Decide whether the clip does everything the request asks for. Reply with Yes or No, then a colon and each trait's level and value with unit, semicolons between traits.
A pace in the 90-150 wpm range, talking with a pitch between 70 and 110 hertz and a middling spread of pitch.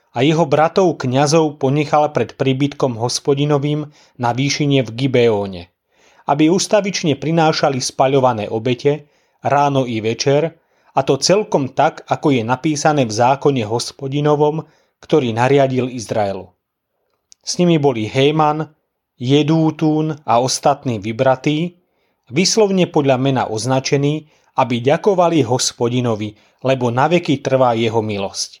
No: slow, 110 wpm; medium, 140 Hz; average, 3.6 semitones